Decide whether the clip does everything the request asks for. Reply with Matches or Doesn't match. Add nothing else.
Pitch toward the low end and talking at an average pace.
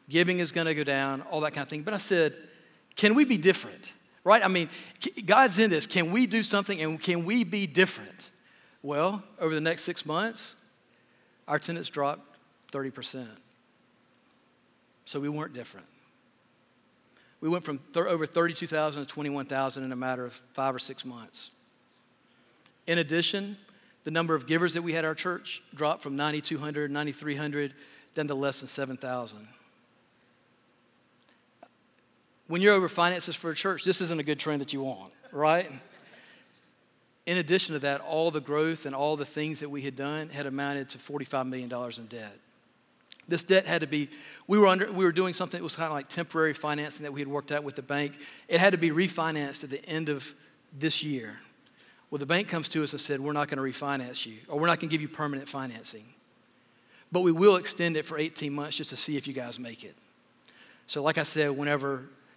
Doesn't match